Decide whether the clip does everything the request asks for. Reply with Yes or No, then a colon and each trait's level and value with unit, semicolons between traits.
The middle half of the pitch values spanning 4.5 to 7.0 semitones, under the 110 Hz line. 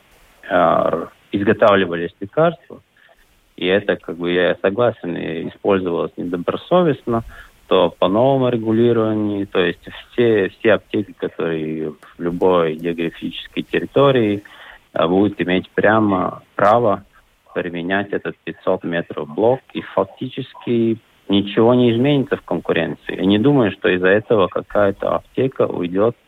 Yes: average, 5.3 semitones; low, 100 Hz